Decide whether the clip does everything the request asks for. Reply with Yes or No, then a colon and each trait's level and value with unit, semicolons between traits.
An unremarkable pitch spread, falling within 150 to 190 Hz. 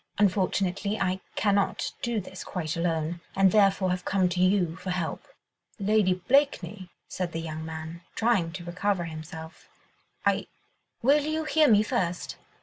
Yes: average, 3.3 semitones; medium, 185 Hz